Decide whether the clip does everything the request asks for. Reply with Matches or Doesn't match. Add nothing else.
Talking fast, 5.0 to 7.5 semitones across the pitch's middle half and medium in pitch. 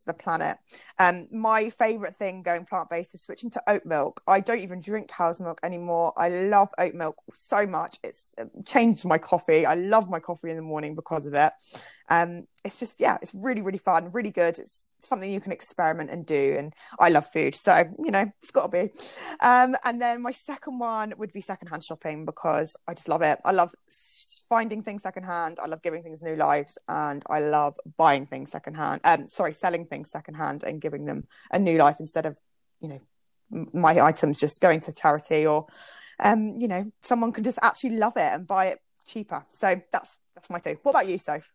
Matches